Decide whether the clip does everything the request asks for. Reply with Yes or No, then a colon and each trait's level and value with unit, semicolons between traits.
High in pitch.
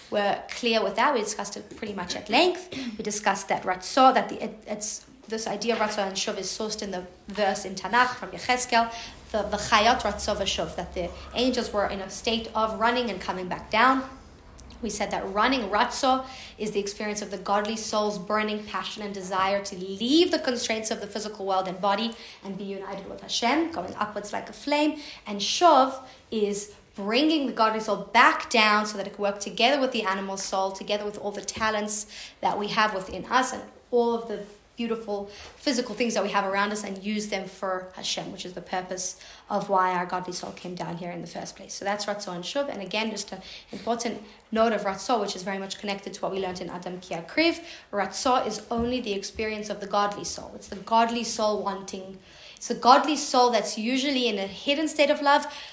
Yes: high, 210 Hz